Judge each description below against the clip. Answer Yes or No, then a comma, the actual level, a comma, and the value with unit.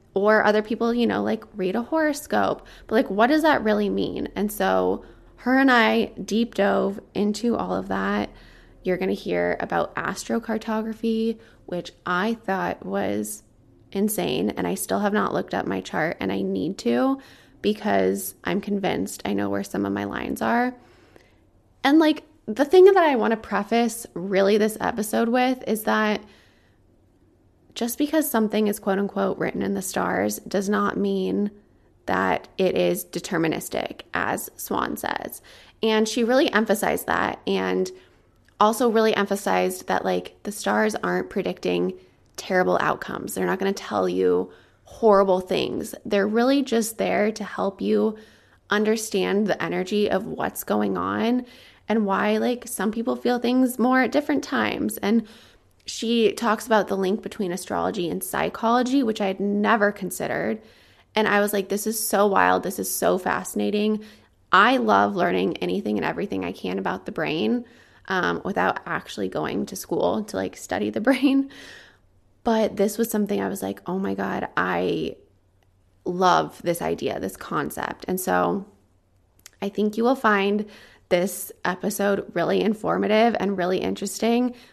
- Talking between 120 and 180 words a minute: Yes, average, 160 wpm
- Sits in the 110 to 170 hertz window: No, high, 205 Hz